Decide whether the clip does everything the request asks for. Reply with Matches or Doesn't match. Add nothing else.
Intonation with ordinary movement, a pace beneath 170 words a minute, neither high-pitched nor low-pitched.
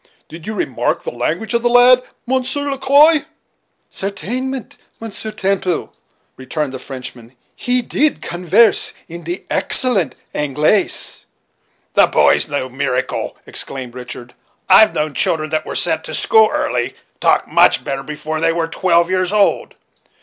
Doesn't match